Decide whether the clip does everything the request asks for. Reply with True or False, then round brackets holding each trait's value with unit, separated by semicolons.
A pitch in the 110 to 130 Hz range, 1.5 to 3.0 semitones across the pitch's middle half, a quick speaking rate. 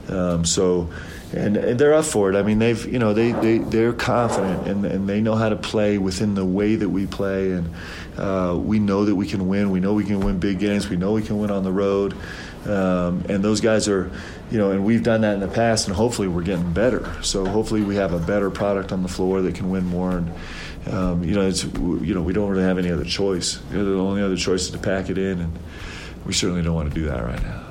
False (95 Hz; 2.5 semitones; 260 wpm)